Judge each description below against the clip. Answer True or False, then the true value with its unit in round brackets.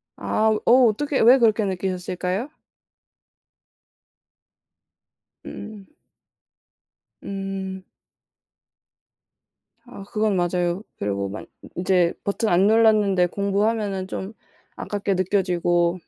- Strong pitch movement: False (2.9 semitones)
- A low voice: False (195 Hz)